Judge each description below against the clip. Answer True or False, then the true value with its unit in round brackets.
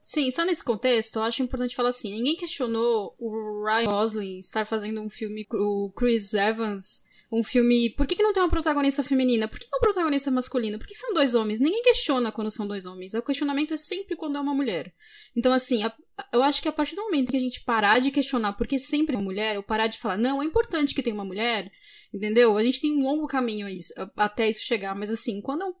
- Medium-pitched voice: False (245 Hz)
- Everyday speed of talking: False (240 wpm)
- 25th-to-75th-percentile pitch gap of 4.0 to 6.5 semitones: True (4.7 semitones)